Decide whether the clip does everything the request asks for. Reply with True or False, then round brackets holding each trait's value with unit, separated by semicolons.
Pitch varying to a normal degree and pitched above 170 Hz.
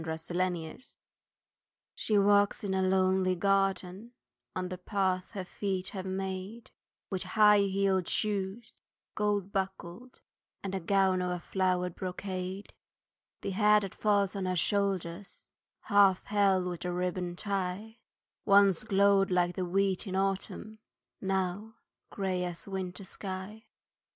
False (1.6 semitones; 190 Hz)